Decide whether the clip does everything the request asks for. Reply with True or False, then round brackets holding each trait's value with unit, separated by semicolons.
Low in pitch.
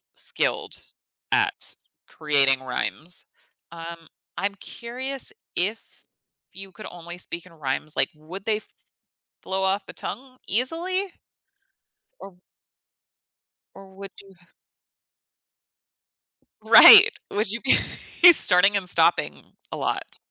False (195 Hz)